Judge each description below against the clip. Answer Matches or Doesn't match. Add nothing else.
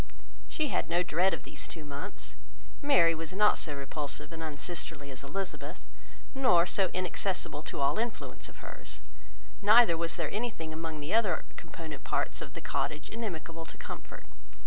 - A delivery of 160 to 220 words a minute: Matches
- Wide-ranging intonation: Doesn't match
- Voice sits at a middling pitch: Matches